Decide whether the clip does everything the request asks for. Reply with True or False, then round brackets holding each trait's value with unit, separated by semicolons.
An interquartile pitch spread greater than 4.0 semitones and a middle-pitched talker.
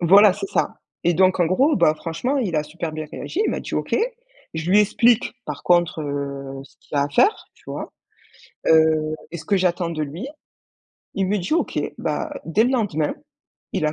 True (4.9 semitones; 175 Hz)